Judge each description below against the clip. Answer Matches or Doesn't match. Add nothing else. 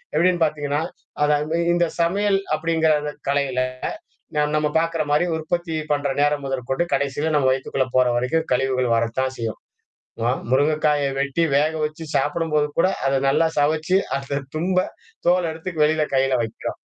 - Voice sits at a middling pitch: Matches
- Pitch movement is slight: Doesn't match